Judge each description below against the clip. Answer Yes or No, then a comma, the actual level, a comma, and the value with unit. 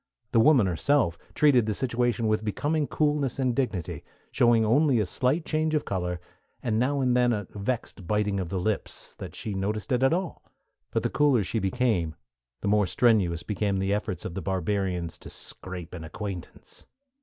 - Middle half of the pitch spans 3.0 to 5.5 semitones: Yes, average, 5.0 semitones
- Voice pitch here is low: Yes, low, 110 Hz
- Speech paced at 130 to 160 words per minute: No, average, 185 wpm